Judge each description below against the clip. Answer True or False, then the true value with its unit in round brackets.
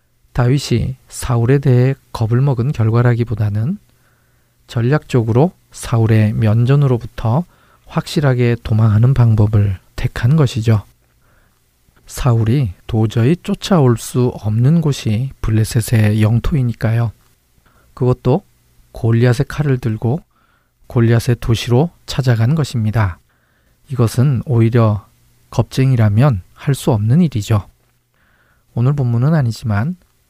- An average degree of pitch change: True (3.0 semitones)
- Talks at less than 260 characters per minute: True (250 characters per minute)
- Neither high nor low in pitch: False (120 Hz)